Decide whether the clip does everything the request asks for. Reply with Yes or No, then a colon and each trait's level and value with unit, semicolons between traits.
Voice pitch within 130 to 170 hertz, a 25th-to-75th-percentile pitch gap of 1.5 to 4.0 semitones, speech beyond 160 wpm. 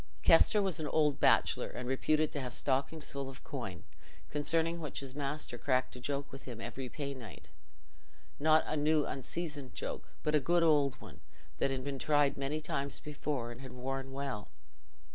Yes: medium, 140 Hz; narrow, 2.4 semitones; average, 180 wpm